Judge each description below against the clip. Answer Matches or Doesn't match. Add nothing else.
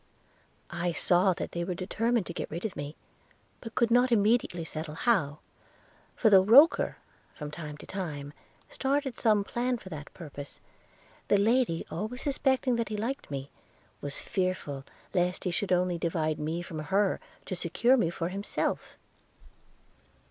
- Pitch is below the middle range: Doesn't match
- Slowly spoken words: Doesn't match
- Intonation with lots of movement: Matches